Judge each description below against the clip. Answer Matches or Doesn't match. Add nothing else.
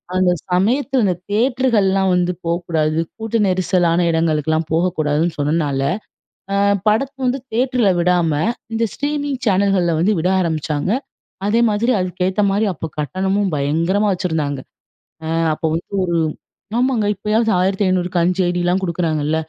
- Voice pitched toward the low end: Doesn't match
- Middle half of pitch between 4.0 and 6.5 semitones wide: Matches